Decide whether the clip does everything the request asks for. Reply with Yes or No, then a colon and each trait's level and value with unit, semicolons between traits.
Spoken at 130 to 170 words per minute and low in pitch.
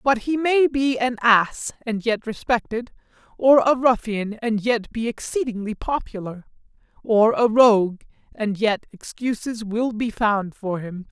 No: average, 150 wpm; high, 230 Hz